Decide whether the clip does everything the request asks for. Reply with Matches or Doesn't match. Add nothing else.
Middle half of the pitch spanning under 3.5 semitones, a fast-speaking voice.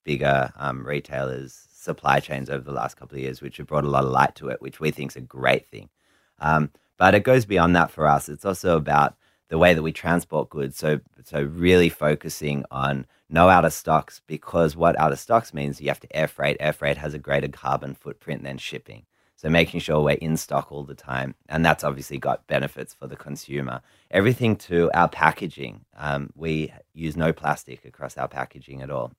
Matches